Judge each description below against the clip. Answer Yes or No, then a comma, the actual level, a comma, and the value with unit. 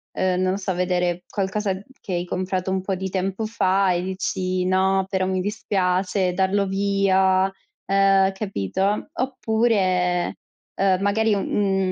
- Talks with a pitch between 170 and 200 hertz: Yes, high, 190 Hz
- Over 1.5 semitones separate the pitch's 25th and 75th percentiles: No, narrow, 1.2 semitones